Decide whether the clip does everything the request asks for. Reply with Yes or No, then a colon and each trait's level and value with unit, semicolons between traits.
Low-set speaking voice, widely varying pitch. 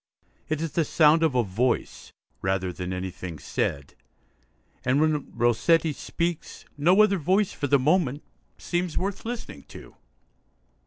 No: medium, 150 Hz; wide, 6.7 semitones